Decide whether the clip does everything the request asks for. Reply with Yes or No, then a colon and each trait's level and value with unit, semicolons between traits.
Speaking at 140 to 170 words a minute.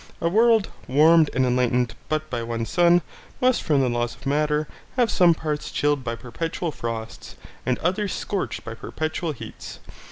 Yes: average, 165 wpm